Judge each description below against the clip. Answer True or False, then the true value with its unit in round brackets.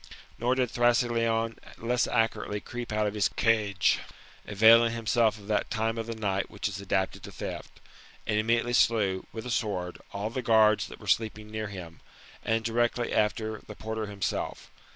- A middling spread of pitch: False (1.9 semitones)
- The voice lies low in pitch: True (110 Hz)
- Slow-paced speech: False (175 wpm)